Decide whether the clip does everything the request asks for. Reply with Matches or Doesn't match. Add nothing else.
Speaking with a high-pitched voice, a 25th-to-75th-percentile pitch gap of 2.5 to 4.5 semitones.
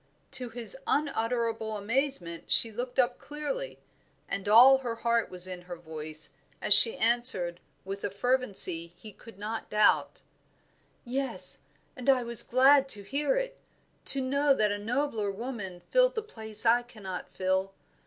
Doesn't match